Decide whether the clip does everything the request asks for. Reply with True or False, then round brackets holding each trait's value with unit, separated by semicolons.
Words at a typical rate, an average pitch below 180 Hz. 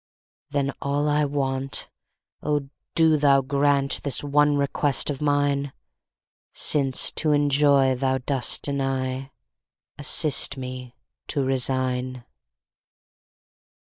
False (80 wpm; 140 Hz)